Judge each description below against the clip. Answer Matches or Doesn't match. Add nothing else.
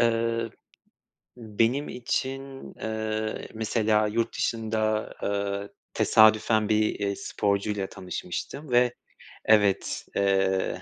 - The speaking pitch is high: Doesn't match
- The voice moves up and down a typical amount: Doesn't match